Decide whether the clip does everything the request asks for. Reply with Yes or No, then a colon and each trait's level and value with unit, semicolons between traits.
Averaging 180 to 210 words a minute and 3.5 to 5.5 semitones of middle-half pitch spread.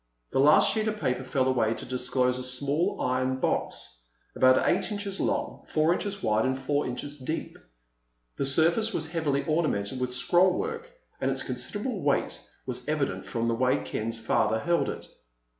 No: average, 170 wpm; average, 5.2 semitones